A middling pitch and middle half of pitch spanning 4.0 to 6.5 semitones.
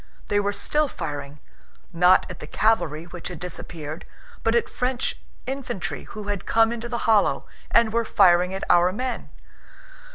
No: high, 205 Hz; average, 5.1 semitones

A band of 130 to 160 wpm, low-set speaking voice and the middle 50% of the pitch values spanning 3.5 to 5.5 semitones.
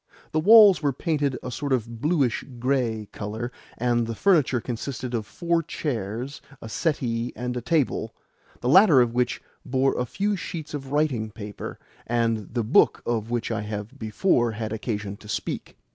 No: average, 170 wpm; low, 125 Hz; average, 4.4 semitones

